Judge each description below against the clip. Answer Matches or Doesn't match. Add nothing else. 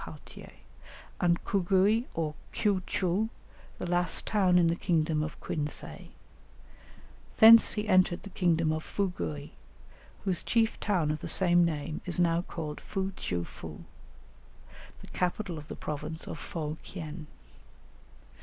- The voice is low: Doesn't match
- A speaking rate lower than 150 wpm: Matches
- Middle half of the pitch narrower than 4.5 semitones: Matches